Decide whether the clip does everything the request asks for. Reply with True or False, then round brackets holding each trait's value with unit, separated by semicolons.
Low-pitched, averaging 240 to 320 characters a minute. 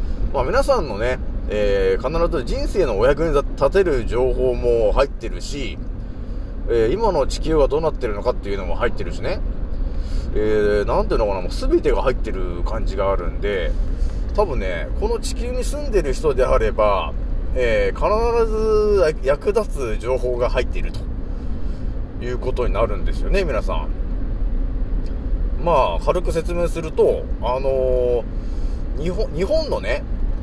True (125 Hz; 290 characters per minute)